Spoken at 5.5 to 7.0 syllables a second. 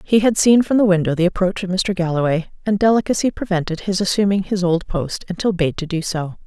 Yes: 5.9 syllables/s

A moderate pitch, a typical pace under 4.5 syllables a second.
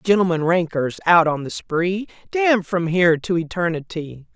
No: medium, 175 Hz; 4.9 syllables/s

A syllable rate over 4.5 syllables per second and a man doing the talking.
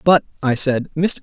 Yes: 4.7 syllables/s; male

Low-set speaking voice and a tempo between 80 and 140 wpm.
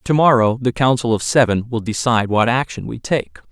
No: low, 120 Hz; fast, 205 wpm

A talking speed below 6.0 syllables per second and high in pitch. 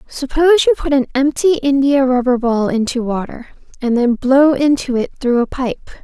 Yes: 4.9 syllables/s; very high, 260 Hz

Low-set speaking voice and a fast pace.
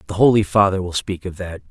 Yes: very low, 95 Hz; fast, 245 wpm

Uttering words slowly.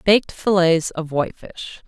Yes: slow, 130 wpm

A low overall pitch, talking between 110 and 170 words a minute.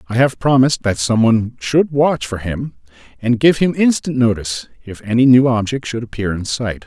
No: low, 120 Hz; average, 190 wpm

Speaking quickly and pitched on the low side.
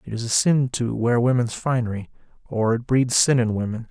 Yes: fast, 215 wpm; low, 120 Hz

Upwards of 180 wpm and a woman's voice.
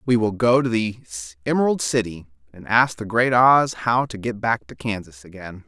No: average, 200 wpm; male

